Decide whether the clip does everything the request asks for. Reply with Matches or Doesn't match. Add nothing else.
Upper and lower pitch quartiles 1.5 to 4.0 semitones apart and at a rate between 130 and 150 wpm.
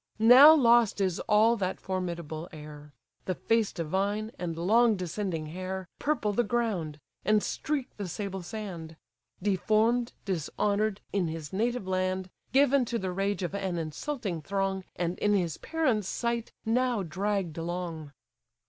Doesn't match